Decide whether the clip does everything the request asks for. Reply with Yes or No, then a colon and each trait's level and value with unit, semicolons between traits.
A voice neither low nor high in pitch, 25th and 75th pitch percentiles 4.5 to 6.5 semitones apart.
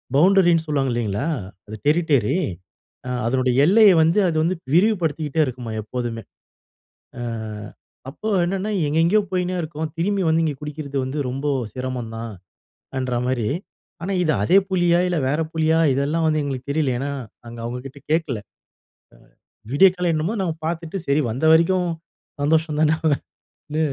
Yes: medium, 155 Hz; average, 4.8 semitones